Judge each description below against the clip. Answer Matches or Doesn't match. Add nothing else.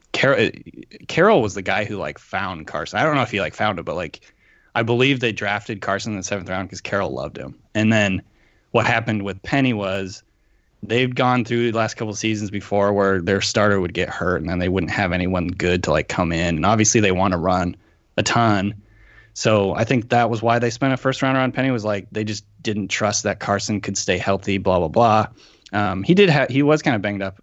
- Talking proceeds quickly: Matches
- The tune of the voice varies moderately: Matches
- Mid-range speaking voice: Doesn't match